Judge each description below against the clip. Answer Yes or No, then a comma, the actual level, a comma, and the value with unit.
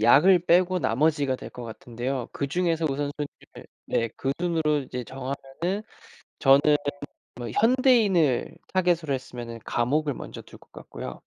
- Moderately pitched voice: Yes, medium, 145 Hz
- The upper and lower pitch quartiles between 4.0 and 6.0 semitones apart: Yes, average, 5.1 semitones